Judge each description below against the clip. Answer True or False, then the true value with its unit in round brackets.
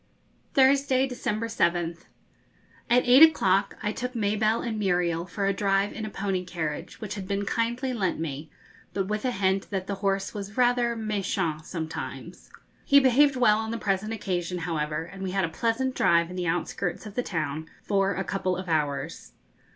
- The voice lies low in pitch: False (195 Hz)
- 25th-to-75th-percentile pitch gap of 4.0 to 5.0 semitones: True (4.4 semitones)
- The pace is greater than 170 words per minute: True (180 wpm)